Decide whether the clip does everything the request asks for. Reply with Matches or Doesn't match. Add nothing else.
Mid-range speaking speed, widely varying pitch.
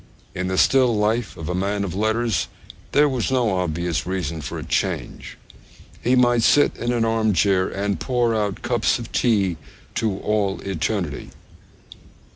Doesn't match